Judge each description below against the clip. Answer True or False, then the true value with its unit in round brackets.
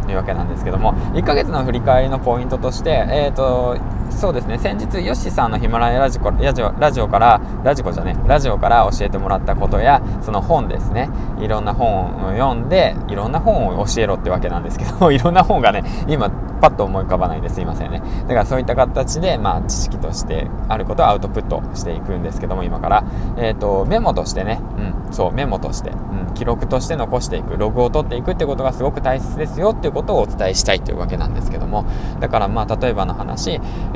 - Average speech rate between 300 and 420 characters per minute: False (455 characters per minute)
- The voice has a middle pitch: False (110 Hz)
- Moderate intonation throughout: True (4.6 semitones)